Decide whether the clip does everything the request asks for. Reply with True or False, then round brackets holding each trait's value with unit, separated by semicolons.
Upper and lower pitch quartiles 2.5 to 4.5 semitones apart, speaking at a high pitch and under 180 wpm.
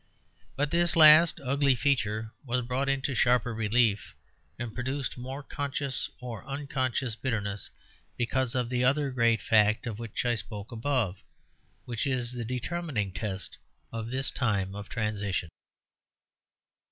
False (3.7 semitones; 125 Hz; 135 wpm)